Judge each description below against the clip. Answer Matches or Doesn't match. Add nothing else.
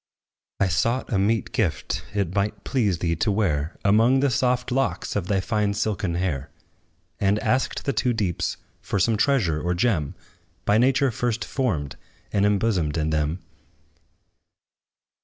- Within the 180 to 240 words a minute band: Doesn't match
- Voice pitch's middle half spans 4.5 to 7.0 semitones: Matches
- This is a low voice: Matches